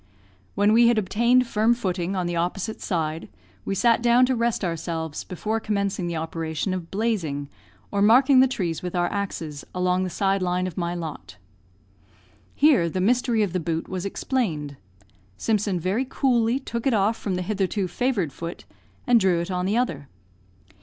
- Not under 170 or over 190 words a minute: Yes, average, 175 wpm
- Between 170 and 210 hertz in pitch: Yes, high, 190 Hz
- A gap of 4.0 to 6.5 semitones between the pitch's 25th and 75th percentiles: Yes, average, 4.9 semitones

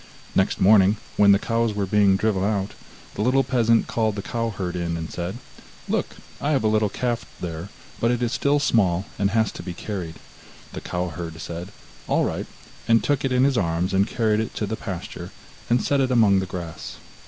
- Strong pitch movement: No, average, 4.0 semitones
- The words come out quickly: Yes, fast, 210 wpm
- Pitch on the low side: Yes, low, 105 Hz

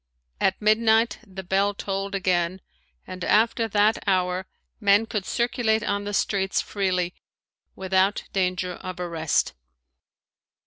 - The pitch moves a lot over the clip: No, narrow, 2.4 semitones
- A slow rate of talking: Yes, slow, 120 wpm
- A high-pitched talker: Yes, high, 195 Hz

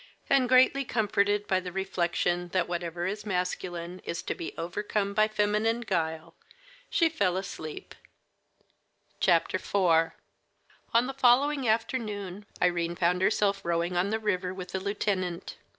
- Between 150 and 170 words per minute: No, slow, 135 wpm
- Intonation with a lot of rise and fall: No, average, 3.4 semitones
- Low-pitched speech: No, high, 190 Hz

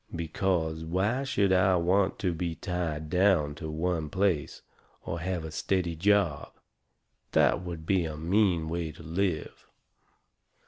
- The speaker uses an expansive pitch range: No, average, 2.9 semitones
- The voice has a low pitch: Yes, very low, 85 Hz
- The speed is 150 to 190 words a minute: No, average, 140 wpm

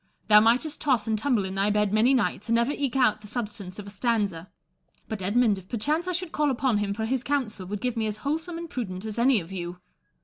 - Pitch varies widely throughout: No, average, 4.3 semitones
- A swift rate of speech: Yes, fast, 245 wpm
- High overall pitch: Yes, high, 220 Hz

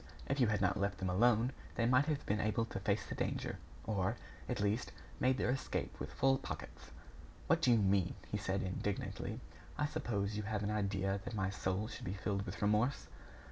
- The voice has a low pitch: Yes, low, 105 Hz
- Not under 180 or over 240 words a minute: Yes, fast, 205 wpm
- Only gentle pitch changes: No, average, 3.7 semitones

